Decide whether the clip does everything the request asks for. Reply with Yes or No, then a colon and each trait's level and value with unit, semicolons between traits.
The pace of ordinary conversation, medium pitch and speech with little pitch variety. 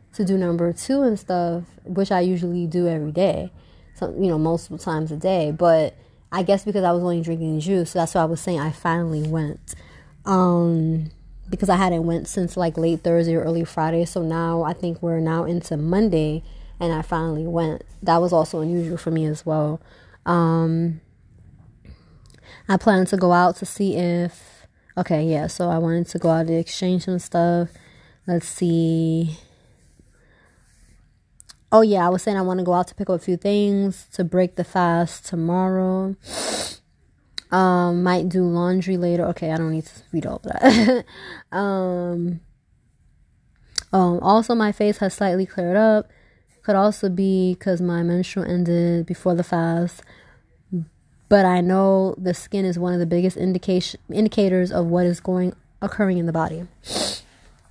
Yes: average, 175 wpm; medium, 175 Hz; narrow, 2.1 semitones